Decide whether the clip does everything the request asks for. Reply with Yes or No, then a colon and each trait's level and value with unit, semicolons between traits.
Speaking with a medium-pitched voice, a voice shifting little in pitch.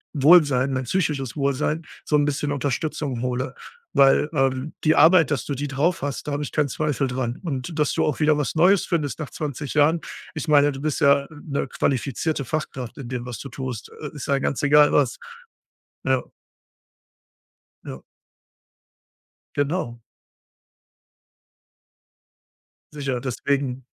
Yes: medium, 145 Hz; narrow, 2.3 semitones